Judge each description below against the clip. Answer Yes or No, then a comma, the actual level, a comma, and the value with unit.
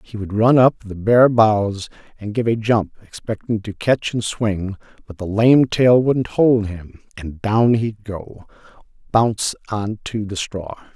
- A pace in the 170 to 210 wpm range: Yes, average, 175 wpm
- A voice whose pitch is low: Yes, low, 110 Hz